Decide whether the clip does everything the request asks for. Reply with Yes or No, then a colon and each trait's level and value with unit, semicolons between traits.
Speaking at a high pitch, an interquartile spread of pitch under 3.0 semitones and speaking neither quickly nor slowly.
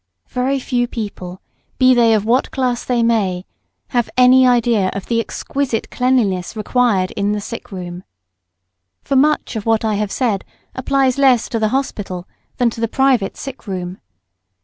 No: high, 230 Hz; average, 4.0 semitones; average, 165 wpm